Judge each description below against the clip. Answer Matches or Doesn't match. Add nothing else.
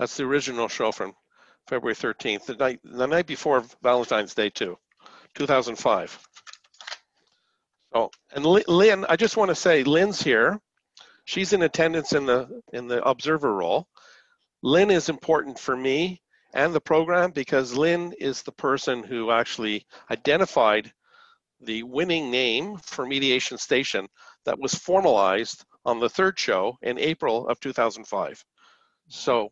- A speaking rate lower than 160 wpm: Matches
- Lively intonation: Matches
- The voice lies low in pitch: Doesn't match